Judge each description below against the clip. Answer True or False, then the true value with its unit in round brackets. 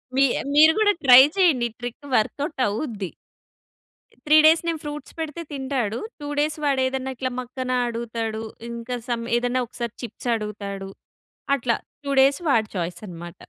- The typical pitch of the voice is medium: False (250 Hz)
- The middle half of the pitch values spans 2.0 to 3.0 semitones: False (4.1 semitones)